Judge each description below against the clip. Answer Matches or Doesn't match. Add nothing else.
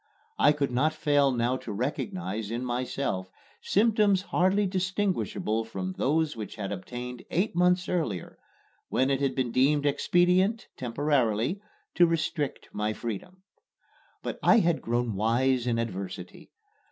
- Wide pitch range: Matches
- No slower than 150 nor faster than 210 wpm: Doesn't match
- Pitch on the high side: Doesn't match